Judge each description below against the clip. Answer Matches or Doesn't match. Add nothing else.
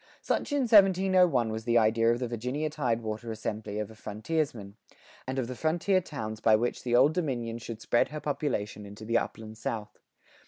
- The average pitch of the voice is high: Doesn't match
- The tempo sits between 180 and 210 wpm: Matches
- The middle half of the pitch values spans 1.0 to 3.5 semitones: Doesn't match